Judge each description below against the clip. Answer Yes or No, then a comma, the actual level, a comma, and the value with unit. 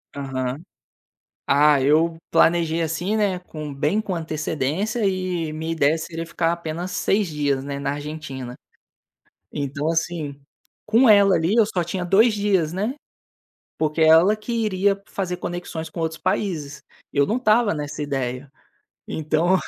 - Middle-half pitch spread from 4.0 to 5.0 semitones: Yes, average, 4.3 semitones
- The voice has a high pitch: No, medium, 165 Hz